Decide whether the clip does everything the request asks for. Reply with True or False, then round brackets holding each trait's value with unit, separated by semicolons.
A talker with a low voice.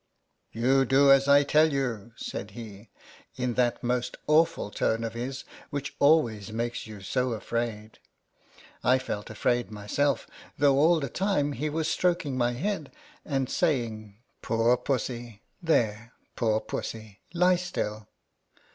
True (125 Hz)